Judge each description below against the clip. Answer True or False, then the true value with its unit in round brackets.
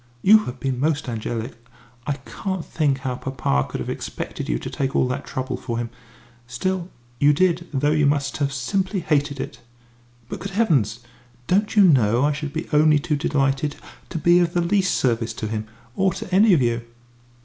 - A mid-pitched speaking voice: True (145 Hz)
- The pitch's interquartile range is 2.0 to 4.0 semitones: False (5.3 semitones)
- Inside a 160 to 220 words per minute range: True (195 wpm)